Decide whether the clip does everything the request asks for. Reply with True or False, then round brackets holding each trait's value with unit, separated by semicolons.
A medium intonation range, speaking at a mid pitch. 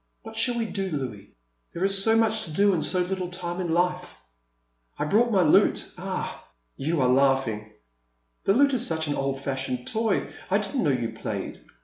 False (7.2 semitones; 175 Hz)